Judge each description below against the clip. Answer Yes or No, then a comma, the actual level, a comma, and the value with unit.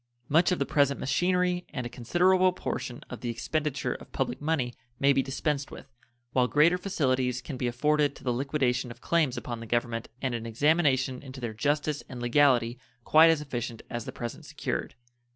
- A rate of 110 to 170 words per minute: No, average, 190 wpm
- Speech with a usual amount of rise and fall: Yes, average, 3.8 semitones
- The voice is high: No, low, 135 Hz